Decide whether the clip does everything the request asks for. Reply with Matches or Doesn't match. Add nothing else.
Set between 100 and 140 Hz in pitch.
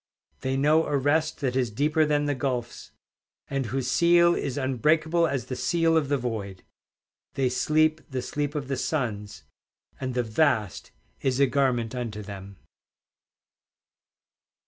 Matches